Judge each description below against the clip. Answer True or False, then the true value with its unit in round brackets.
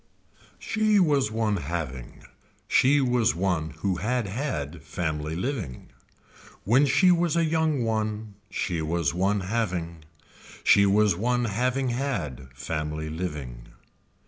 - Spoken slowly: True (120 wpm)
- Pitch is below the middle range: True (100 Hz)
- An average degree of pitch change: False (7.8 semitones)